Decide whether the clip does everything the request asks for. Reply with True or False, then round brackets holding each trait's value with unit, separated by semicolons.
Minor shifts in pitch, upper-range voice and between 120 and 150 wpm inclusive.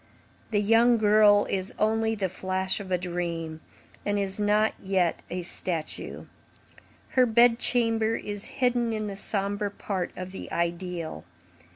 False (3.2 semitones; 200 Hz; 145 wpm)